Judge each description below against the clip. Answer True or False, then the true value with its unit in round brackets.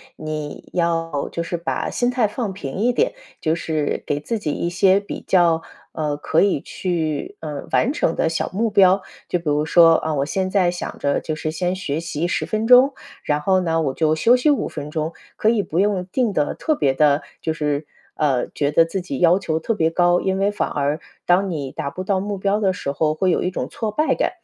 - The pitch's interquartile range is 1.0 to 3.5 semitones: False (4.2 semitones)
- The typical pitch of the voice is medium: True (170 Hz)